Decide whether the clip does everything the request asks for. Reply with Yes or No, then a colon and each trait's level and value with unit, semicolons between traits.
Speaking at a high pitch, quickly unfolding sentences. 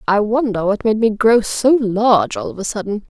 Yes: high, 220 Hz; fast, 225 wpm